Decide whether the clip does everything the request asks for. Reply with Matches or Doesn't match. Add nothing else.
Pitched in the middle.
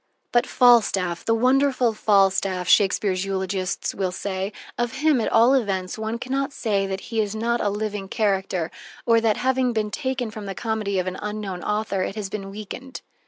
Doesn't match